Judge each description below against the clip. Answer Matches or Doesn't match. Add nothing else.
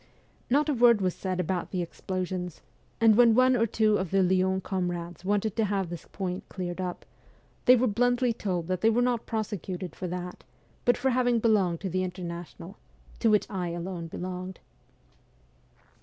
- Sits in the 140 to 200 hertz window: Matches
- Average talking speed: Matches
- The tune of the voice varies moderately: Matches